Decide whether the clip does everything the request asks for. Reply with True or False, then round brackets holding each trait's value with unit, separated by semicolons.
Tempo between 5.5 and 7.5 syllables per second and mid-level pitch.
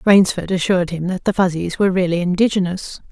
True (6.2 syllables/s; 180 Hz)